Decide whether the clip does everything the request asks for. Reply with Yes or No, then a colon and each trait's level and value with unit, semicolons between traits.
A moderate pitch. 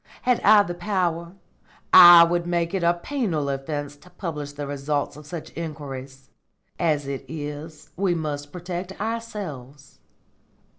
Yes: medium, 165 Hz